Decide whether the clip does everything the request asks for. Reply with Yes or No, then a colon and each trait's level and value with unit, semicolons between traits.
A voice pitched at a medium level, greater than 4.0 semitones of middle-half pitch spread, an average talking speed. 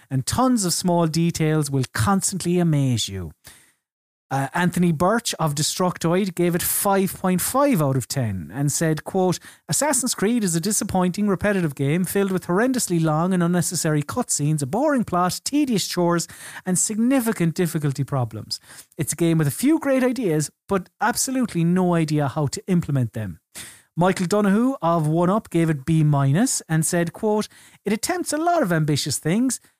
Yes: medium, 175 Hz; average, 5.1 semitones; average, 160 wpm